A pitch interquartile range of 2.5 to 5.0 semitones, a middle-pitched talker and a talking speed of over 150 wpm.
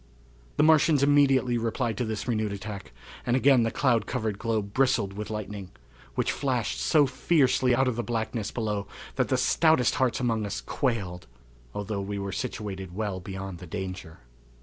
No: average, 4.2 semitones; low, 110 Hz; average, 170 wpm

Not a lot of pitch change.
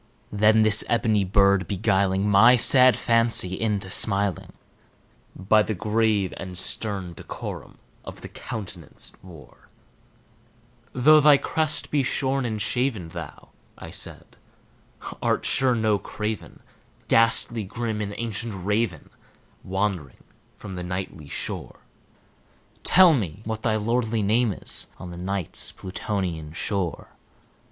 No: average, 3.4 semitones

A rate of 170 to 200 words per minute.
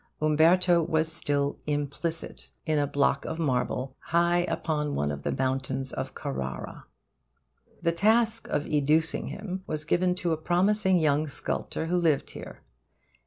No: average, 145 wpm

